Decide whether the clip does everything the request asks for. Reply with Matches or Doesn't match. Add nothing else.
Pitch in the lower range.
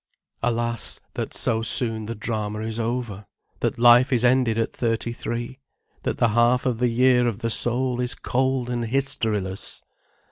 Matches